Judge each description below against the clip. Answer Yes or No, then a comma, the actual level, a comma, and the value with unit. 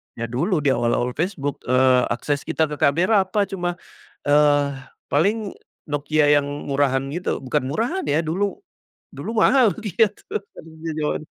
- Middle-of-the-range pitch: Yes, medium, 150 Hz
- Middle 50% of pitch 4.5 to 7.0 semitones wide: Yes, average, 5.1 semitones